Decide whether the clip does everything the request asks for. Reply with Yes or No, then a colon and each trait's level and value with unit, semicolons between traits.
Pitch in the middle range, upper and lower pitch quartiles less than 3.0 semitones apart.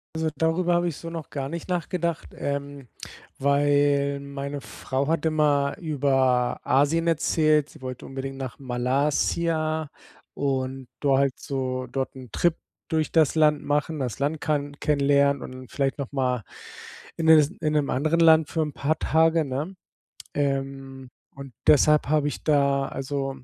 Yes: medium, 145 Hz; narrow, 2.5 semitones